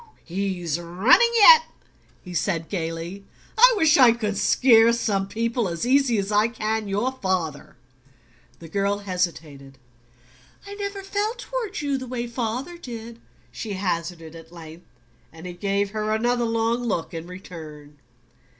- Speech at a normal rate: Yes, average, 145 wpm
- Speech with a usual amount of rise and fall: No, wide, 5.8 semitones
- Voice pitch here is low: No, high, 205 Hz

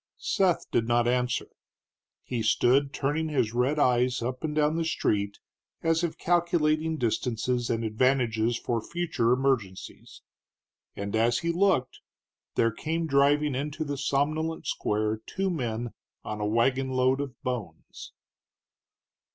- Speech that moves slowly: Yes, slow, 130 wpm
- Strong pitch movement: No, average, 4.7 semitones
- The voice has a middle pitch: No, low, 130 Hz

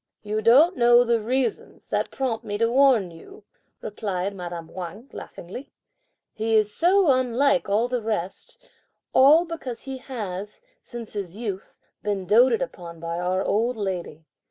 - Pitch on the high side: Yes, high, 225 Hz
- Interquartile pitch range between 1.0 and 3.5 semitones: No, average, 4.8 semitones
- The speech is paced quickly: No, average, 155 wpm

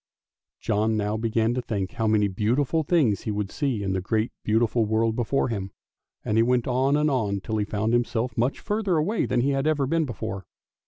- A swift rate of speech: Yes, fast, 210 wpm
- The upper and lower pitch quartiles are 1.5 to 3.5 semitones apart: No, average, 4.0 semitones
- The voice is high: No, low, 115 Hz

